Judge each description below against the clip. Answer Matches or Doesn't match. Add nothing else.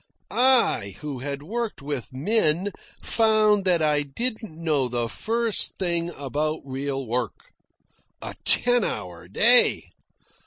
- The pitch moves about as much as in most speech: Doesn't match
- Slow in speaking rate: Matches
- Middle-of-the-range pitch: Matches